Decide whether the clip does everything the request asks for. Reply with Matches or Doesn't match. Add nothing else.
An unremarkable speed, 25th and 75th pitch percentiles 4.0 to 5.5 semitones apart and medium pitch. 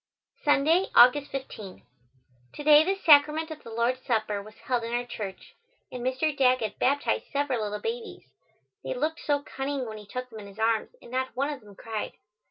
Doesn't match